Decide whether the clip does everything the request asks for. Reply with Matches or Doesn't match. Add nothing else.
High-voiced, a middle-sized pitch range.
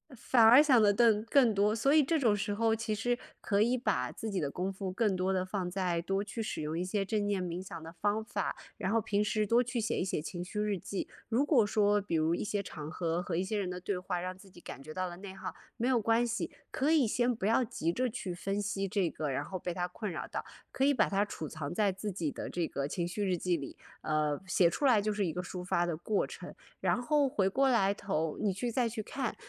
Matches